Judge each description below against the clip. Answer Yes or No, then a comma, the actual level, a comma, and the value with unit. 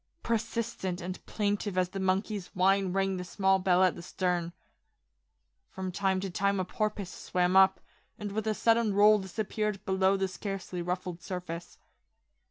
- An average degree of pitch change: No, narrow, 2.0 semitones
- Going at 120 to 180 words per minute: Yes, average, 160 wpm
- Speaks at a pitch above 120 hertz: Yes, high, 190 Hz